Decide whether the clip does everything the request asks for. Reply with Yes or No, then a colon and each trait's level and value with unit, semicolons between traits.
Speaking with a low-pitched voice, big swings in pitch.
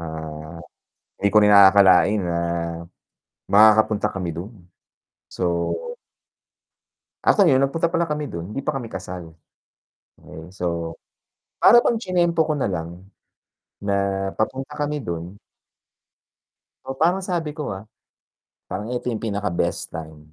Yes: low, 100 Hz; wide, 8.5 semitones